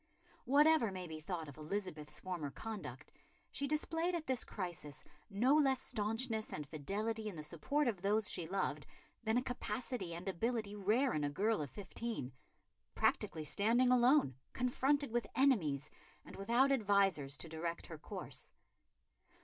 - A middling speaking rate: Yes, average, 150 wpm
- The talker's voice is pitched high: Yes, high, 210 Hz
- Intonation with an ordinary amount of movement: No, wide, 7.1 semitones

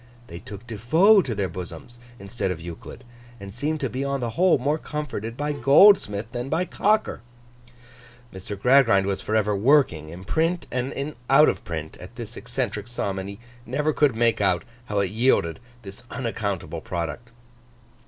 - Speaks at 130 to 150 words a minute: No, average, 175 wpm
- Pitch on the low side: Yes, low, 115 Hz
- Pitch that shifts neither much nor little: No, wide, 6.0 semitones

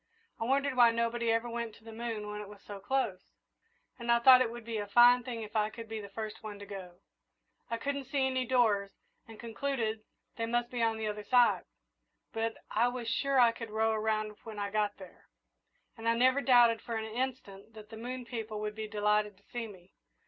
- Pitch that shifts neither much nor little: No, narrow, 2.2 semitones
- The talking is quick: Yes, fast, 220 wpm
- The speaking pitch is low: No, high, 225 Hz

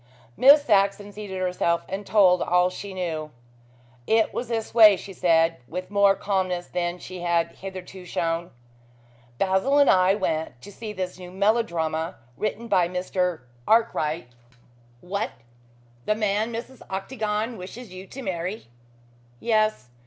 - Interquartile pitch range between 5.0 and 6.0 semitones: No, average, 3.3 semitones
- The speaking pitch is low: No, high, 190 Hz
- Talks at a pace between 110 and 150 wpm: Yes, average, 140 wpm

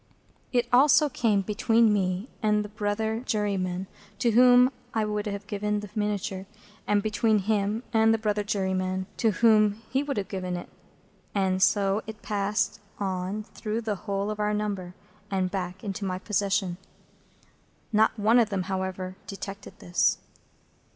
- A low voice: No, high, 205 Hz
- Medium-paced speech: Yes, average, 155 wpm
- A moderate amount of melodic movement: No, narrow, 2.1 semitones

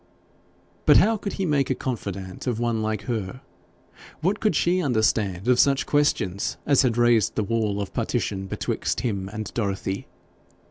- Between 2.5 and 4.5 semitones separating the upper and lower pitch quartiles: No, wide, 5.5 semitones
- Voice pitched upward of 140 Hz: No, low, 115 Hz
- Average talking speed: Yes, average, 160 wpm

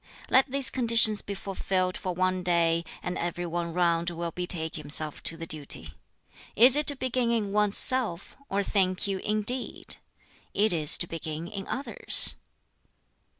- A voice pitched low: No, medium, 185 Hz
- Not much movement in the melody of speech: No, average, 4.1 semitones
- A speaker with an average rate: Yes, average, 155 wpm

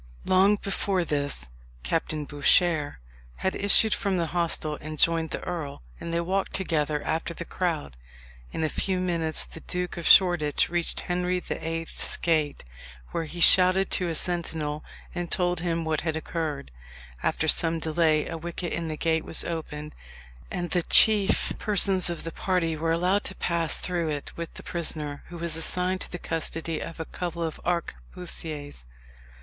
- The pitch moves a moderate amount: No, narrow, 2.2 semitones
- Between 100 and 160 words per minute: No, average, 170 wpm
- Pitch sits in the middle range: Yes, medium, 165 Hz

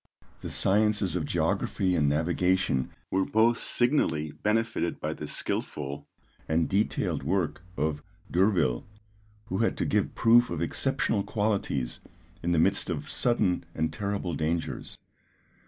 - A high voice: No, very low, 90 Hz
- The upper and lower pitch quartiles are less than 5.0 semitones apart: No, average, 5.3 semitones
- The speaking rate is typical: No, slow, 130 wpm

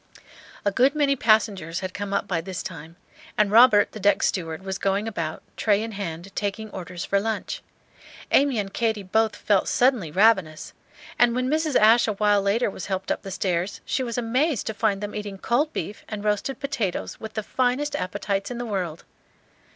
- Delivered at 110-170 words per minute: No, average, 190 wpm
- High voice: Yes, high, 205 Hz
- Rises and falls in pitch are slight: No, average, 3.4 semitones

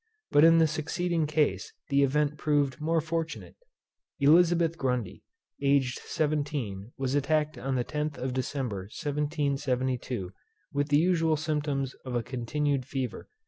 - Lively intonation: No, average, 3.0 semitones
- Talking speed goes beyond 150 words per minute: No, slow, 135 wpm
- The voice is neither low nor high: Yes, medium, 145 Hz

